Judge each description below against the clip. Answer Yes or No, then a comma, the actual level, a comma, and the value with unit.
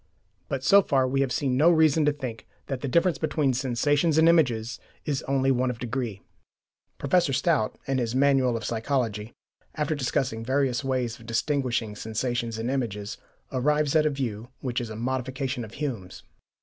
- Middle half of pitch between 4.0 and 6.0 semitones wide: No, average, 3.3 semitones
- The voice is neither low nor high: No, low, 130 Hz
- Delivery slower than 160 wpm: No, average, 175 wpm